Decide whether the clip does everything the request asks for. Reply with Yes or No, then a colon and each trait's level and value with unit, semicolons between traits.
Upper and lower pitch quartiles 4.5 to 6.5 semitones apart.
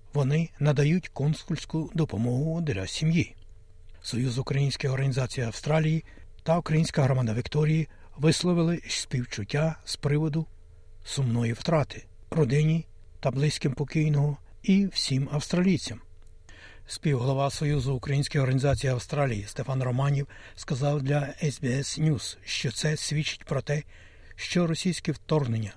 Yes: average, 5.0 semitones